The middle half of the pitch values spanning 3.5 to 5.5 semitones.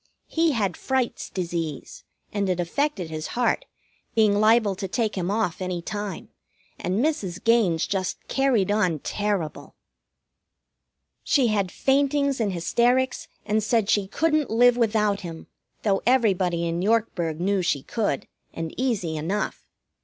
Yes: average, 4.8 semitones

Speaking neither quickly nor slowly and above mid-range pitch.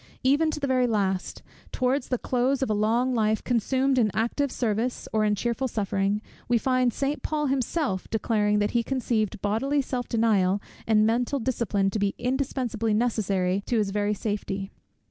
Yes: average, 170 wpm; high, 230 Hz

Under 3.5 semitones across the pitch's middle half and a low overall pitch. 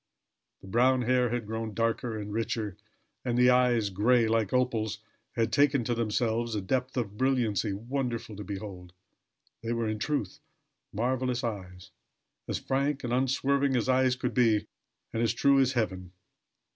Yes: average, 3.0 semitones; low, 115 Hz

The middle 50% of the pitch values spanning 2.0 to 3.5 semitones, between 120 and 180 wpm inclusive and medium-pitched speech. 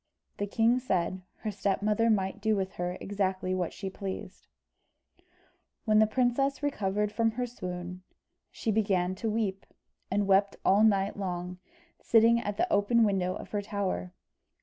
No: average, 2.7 semitones; average, 150 wpm; high, 200 Hz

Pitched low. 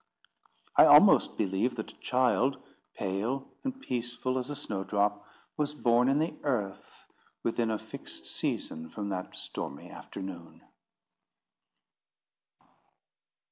Yes: low, 115 Hz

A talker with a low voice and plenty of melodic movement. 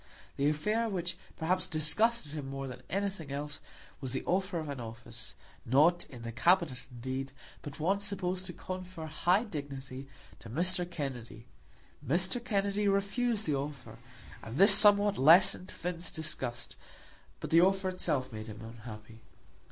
No: medium, 160 Hz; wide, 6.1 semitones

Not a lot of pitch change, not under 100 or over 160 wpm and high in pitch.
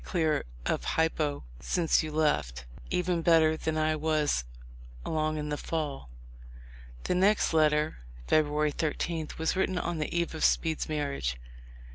No: narrow, 1.4 semitones; average, 145 wpm; medium, 155 Hz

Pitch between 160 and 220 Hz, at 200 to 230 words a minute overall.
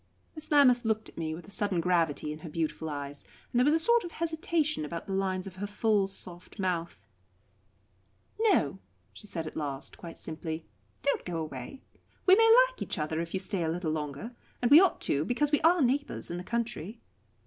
Yes: high, 190 Hz; fast, 205 wpm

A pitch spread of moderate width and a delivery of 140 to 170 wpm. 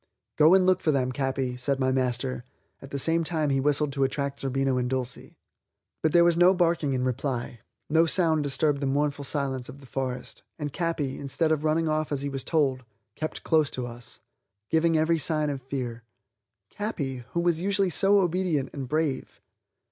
No: average, 3.5 semitones; average, 190 wpm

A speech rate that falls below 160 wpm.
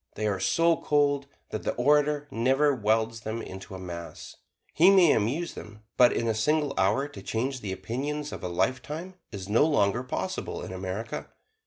No: average, 180 wpm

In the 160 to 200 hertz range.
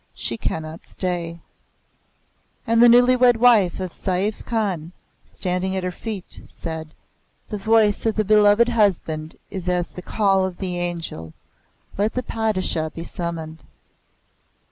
Yes: medium, 185 Hz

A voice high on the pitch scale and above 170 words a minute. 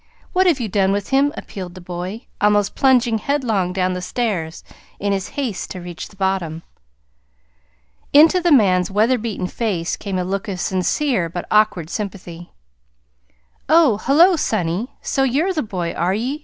No: high, 205 Hz; average, 165 wpm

